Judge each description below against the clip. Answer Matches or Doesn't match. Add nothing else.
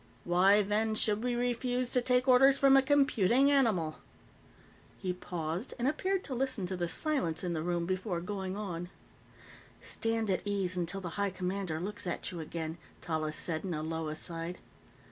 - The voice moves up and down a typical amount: Doesn't match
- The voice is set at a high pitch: Matches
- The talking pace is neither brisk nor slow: Matches